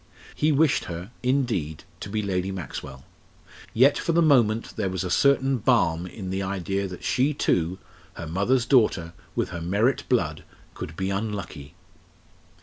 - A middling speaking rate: Yes, average, 155 wpm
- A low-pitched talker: Yes, low, 100 Hz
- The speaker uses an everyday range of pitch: No, wide, 6.3 semitones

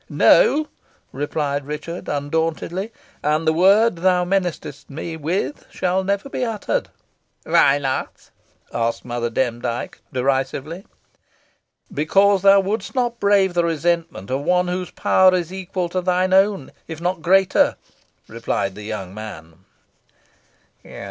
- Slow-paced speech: Yes, slow, 125 wpm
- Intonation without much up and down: No, average, 5.1 semitones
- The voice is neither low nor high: Yes, medium, 170 Hz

